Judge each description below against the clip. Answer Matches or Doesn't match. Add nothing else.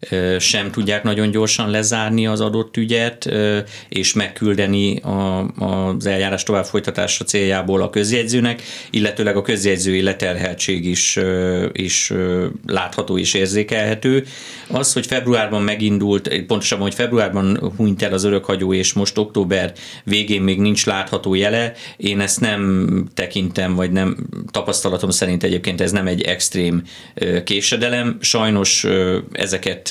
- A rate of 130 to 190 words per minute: Doesn't match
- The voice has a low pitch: Matches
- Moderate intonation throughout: Doesn't match